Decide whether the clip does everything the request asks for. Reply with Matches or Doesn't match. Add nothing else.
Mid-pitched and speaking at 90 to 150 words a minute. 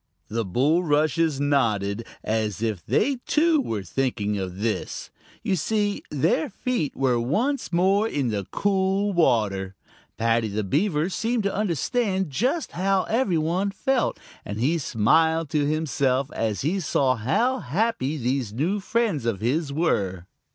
Matches